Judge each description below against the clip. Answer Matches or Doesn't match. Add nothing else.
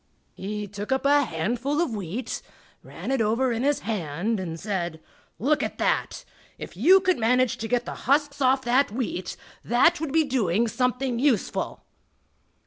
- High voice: Matches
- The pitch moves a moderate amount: Matches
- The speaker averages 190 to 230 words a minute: Doesn't match